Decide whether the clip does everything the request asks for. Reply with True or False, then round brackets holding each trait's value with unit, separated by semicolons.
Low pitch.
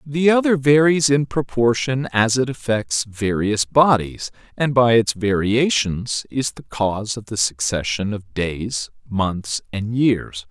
True (115 Hz)